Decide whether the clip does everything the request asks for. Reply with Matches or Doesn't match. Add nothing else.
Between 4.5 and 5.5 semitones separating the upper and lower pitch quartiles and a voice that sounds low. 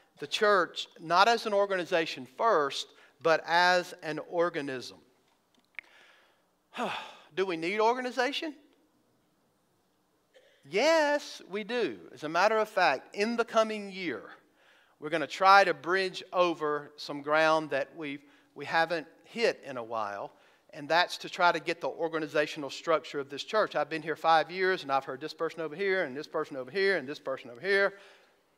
Doesn't match